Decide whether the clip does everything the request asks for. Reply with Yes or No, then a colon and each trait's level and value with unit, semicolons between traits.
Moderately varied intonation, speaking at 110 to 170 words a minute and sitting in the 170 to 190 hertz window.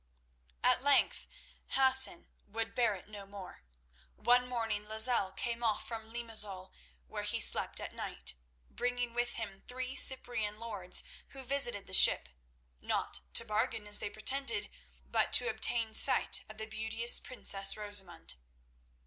No: average, 3.1 semitones; average, 140 wpm; high, 220 Hz